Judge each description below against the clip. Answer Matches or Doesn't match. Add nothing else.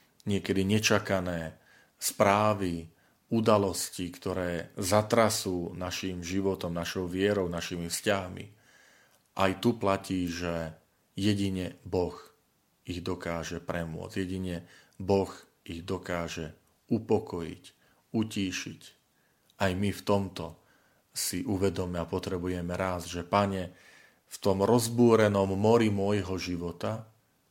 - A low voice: Matches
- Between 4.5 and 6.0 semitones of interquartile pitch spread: Doesn't match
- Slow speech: Matches